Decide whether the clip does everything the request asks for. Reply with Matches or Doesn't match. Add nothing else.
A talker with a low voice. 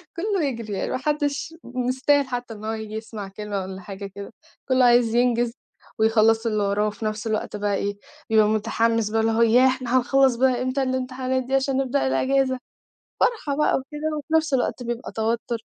Doesn't match